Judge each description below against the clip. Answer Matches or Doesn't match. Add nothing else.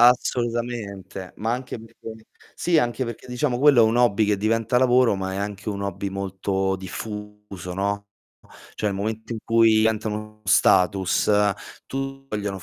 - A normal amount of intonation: Matches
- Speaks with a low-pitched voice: Matches